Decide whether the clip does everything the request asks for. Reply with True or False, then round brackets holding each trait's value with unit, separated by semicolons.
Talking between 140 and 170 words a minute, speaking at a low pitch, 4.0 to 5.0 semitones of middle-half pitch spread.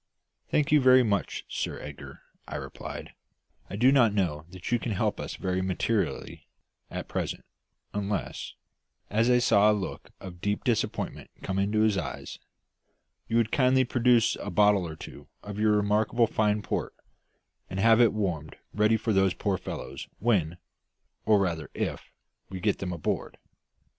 False (165 wpm; 105 Hz; 3.3 semitones)